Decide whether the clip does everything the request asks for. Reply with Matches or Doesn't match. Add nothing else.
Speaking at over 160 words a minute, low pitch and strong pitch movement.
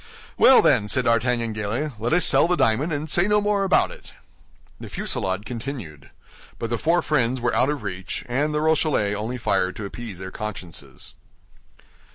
Matches